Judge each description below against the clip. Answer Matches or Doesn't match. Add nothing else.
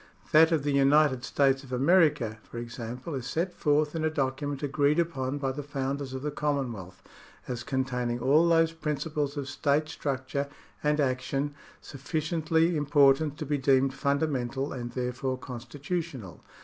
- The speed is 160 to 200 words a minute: Doesn't match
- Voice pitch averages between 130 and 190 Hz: Matches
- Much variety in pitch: Doesn't match